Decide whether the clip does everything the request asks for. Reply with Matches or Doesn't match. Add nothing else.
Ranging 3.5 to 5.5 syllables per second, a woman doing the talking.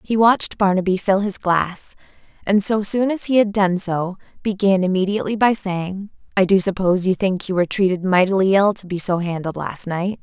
Matches